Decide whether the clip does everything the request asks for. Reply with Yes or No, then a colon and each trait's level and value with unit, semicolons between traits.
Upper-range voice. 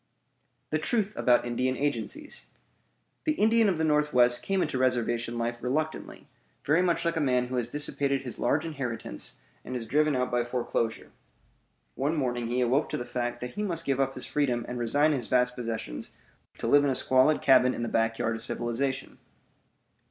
No: low, 130 Hz